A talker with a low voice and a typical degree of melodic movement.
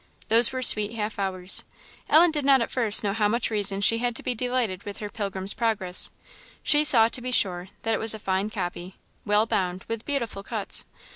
No: high, 215 Hz; average, 3.4 semitones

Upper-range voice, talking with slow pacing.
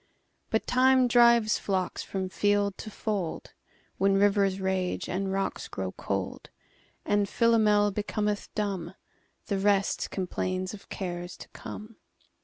Yes: high, 200 Hz; slow, 110 wpm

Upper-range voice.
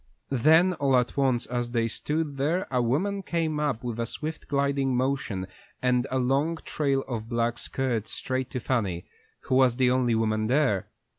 No: low, 130 Hz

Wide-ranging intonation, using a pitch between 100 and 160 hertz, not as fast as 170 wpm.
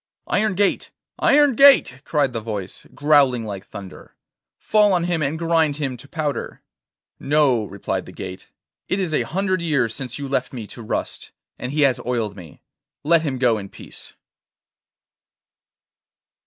Yes: wide, 6.2 semitones; medium, 140 Hz; average, 155 wpm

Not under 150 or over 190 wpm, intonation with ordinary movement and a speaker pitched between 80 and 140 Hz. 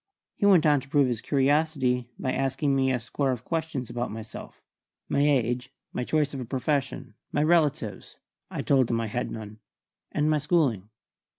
Yes: average, 180 wpm; average, 3.3 semitones; low, 135 Hz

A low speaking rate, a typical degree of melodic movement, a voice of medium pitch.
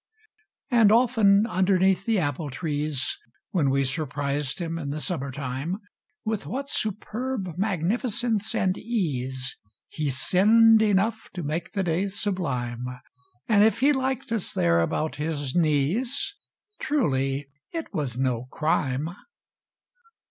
No: slow, 130 wpm; wide, 7.7 semitones; medium, 175 Hz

